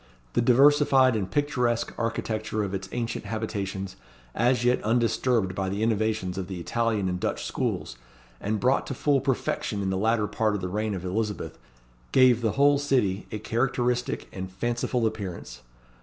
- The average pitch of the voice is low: Yes, low, 110 Hz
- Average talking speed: Yes, average, 165 wpm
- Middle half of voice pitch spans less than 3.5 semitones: No, average, 3.9 semitones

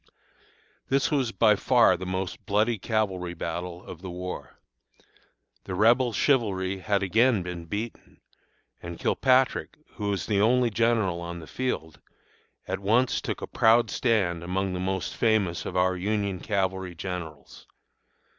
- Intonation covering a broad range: No, average, 3.8 semitones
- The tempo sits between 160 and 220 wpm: No, average, 145 wpm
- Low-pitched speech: Yes, very low, 95 Hz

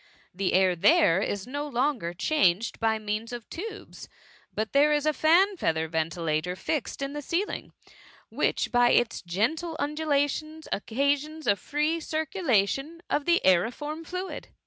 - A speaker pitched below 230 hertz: No, very high, 280 Hz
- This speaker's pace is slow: No, average, 150 wpm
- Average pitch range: No, wide, 7.6 semitones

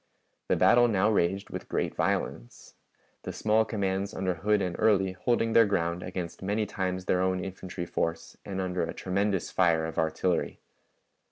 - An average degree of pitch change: No, narrow, 2.3 semitones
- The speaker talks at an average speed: Yes, average, 165 wpm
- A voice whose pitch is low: Yes, very low, 95 Hz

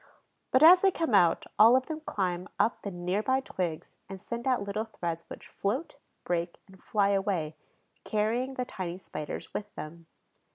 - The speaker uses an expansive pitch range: Yes, wide, 5.9 semitones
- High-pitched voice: Yes, high, 200 Hz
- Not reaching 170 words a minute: No, average, 175 wpm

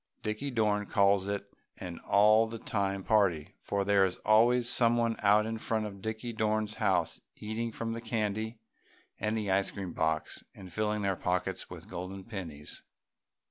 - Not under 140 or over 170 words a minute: Yes, average, 165 wpm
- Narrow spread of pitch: Yes, narrow, 2.2 semitones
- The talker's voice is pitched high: No, low, 105 Hz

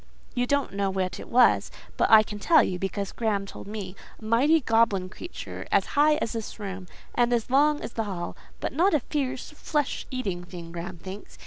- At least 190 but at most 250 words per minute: Yes, fast, 205 wpm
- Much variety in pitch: Yes, wide, 5.7 semitones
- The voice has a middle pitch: No, high, 220 Hz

